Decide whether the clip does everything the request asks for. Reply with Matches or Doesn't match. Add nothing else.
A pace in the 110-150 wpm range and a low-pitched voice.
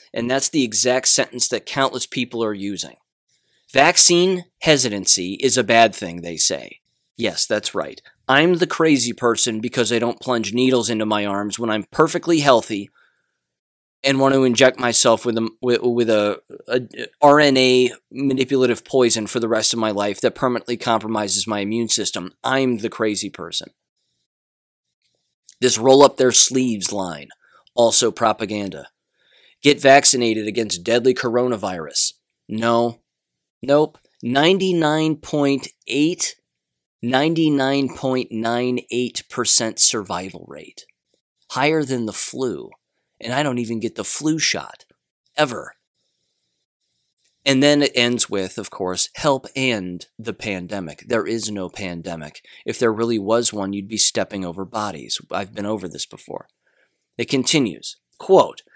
Matches